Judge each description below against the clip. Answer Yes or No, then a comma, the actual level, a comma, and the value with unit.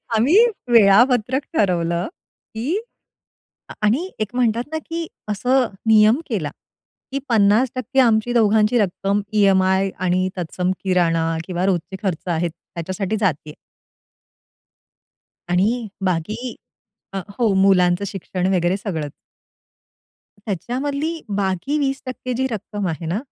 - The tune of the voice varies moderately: Yes, average, 5.0 semitones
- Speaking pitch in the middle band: No, high, 205 Hz